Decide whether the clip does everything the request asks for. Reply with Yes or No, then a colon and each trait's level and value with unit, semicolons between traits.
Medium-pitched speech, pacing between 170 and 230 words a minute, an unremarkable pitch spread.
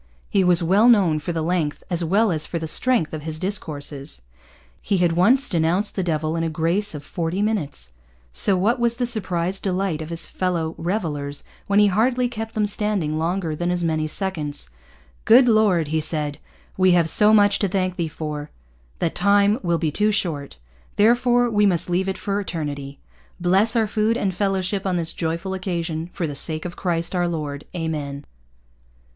Yes: medium, 175 Hz; average, 185 wpm; average, 4.2 semitones